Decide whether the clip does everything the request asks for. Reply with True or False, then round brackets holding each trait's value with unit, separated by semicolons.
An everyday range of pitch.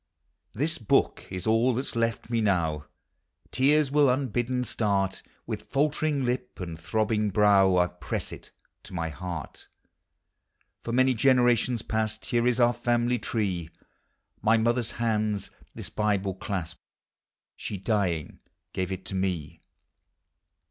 True (4.5 semitones)